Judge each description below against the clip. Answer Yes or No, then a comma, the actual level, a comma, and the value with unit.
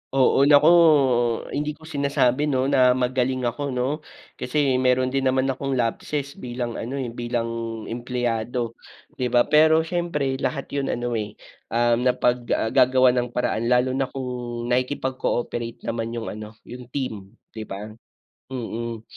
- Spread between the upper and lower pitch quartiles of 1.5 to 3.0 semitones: Yes, narrow, 2.4 semitones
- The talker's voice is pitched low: Yes, low, 125 Hz